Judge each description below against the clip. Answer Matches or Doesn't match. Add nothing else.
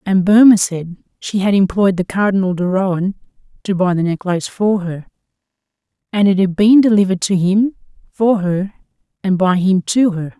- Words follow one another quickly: Doesn't match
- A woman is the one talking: Matches